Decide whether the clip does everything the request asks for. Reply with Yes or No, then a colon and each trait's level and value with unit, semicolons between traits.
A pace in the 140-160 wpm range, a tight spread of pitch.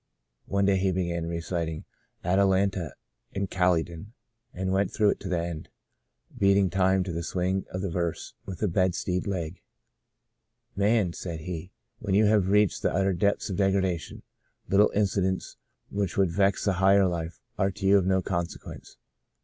No: average, 180 wpm; narrow, 2.2 semitones